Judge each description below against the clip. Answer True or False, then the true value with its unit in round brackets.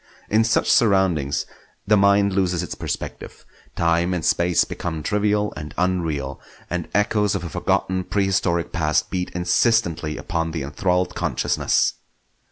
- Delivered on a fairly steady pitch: False (3.3 semitones)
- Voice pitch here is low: True (90 Hz)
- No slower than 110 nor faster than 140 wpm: True (135 wpm)